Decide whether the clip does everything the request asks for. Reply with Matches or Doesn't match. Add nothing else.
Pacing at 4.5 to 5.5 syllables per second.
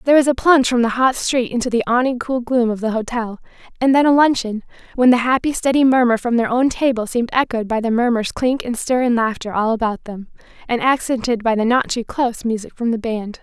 Doesn't match